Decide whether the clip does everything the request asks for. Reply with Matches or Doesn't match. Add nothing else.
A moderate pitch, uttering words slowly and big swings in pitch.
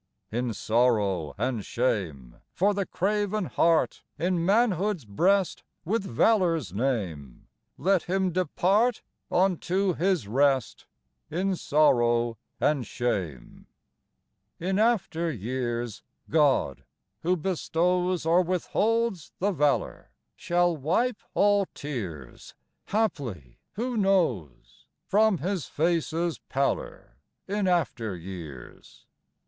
Matches